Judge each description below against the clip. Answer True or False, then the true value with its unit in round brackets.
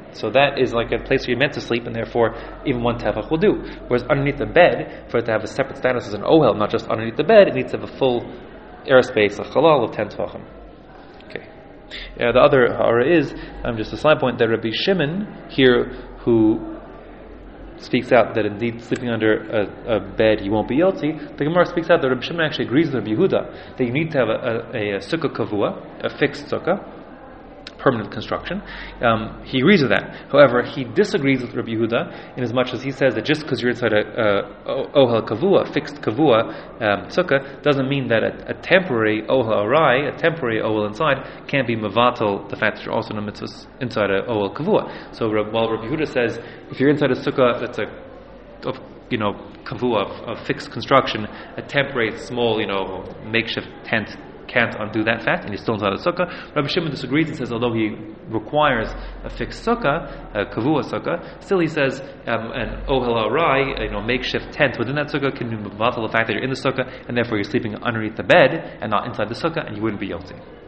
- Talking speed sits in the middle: False (215 wpm)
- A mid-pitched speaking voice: False (120 Hz)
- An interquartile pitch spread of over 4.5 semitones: False (3.9 semitones)